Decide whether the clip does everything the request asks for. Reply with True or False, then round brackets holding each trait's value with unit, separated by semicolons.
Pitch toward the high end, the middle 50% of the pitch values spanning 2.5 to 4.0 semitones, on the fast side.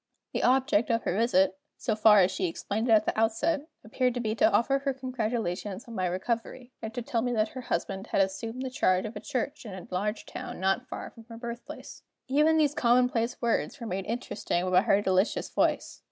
True (230 Hz; 3.6 semitones; 215 wpm)